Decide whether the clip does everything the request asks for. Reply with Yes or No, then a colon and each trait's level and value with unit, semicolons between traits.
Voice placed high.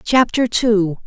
Yes: high, 220 Hz